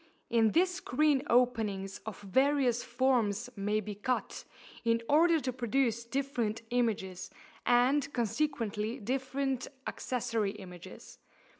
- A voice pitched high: Yes, high, 240 Hz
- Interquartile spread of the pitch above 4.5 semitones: No, average, 4.1 semitones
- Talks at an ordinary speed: No, slow, 110 wpm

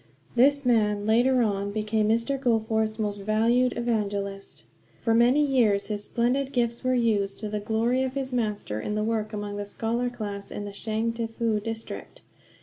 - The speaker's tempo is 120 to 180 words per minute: Yes, average, 165 wpm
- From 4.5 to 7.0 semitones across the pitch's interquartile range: No, narrow, 2.5 semitones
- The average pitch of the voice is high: Yes, high, 225 Hz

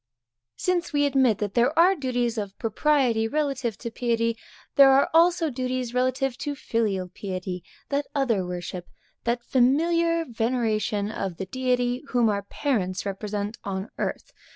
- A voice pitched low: No, high, 240 Hz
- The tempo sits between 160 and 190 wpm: No, average, 150 wpm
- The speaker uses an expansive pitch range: No, average, 4.8 semitones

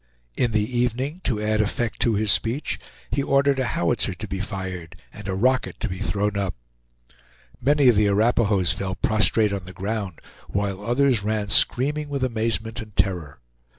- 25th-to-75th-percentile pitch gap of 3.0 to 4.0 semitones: Yes, average, 3.7 semitones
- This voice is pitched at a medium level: No, low, 110 Hz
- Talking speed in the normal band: Yes, average, 175 wpm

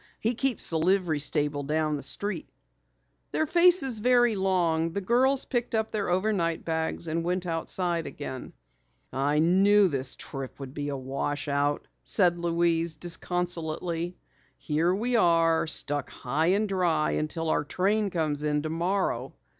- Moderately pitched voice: Yes, medium, 170 Hz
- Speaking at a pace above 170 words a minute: No, average, 145 wpm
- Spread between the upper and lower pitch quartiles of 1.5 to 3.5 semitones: No, average, 4.4 semitones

